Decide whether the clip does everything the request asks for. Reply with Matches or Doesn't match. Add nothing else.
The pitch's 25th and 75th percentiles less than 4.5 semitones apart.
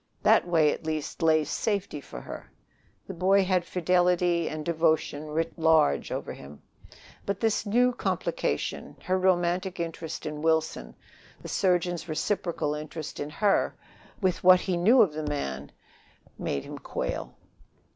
Matches